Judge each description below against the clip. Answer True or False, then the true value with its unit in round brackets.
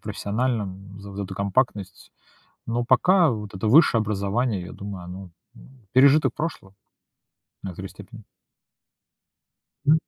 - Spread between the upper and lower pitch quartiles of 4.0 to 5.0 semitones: True (4.3 semitones)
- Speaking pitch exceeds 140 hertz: False (105 Hz)